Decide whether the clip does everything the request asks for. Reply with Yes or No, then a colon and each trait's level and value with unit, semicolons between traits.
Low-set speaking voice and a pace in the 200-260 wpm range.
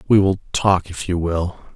Yes: very low, 90 Hz; fast, 205 wpm